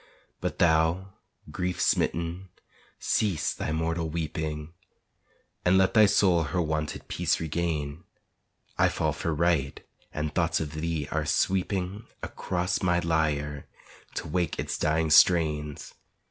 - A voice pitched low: Yes, very low, 80 Hz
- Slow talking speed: Yes, slow, 125 wpm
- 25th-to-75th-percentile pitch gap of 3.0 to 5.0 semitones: No, narrow, 2.4 semitones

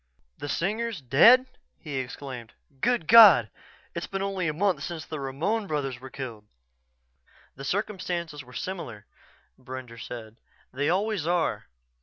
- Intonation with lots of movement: Yes, wide, 6.9 semitones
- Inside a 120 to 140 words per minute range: Yes, slow, 135 wpm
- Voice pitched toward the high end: No, medium, 155 Hz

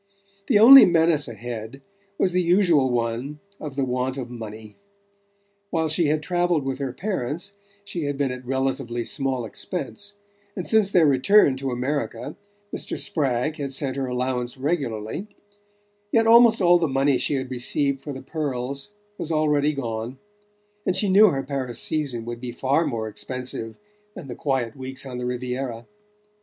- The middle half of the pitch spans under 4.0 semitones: No, average, 4.5 semitones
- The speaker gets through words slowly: No, average, 165 wpm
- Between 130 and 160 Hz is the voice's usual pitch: Yes, low, 135 Hz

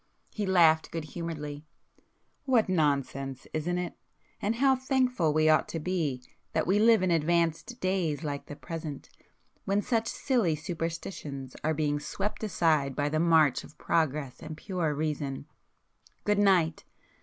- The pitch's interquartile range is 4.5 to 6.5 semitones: No, average, 4.0 semitones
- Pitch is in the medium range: Yes, medium, 165 Hz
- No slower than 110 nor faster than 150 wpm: Yes, average, 145 wpm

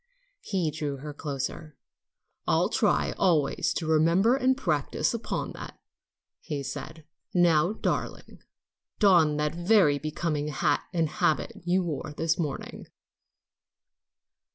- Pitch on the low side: No, medium, 155 Hz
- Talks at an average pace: No, slow, 115 wpm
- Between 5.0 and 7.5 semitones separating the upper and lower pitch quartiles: No, average, 2.9 semitones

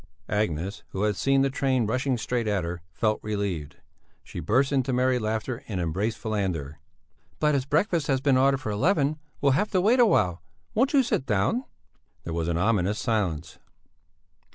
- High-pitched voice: No, low, 115 Hz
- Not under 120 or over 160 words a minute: No, average, 175 wpm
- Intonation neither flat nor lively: No, wide, 6.1 semitones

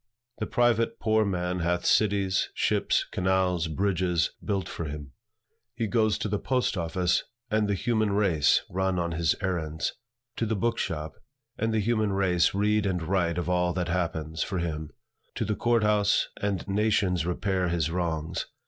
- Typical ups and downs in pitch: Yes, average, 3.6 semitones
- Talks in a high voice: No, very low, 95 Hz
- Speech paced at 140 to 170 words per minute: Yes, average, 165 wpm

